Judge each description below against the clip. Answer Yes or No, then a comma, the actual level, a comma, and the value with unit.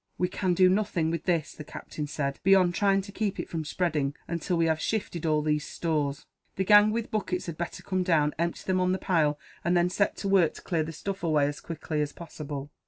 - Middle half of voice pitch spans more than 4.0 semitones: No, average, 3.5 semitones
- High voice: No, medium, 170 Hz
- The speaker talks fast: Yes, fast, 235 wpm